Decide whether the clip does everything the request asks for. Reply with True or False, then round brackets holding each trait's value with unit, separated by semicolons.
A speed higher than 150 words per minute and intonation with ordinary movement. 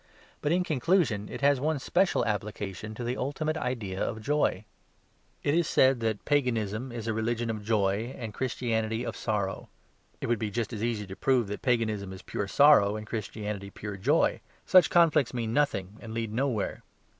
True (180 wpm; 4.0 semitones)